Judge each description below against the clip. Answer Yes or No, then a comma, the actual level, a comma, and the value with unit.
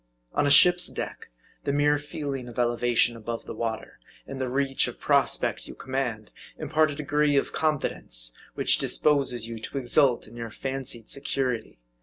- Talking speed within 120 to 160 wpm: No, average, 170 wpm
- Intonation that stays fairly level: No, average, 3.6 semitones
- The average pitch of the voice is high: No, low, 135 Hz